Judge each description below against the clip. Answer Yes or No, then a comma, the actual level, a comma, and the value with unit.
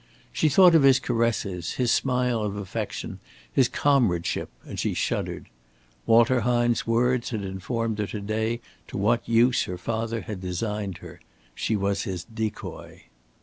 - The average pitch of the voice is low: Yes, low, 115 Hz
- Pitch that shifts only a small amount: No, average, 3.4 semitones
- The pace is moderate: Yes, average, 150 wpm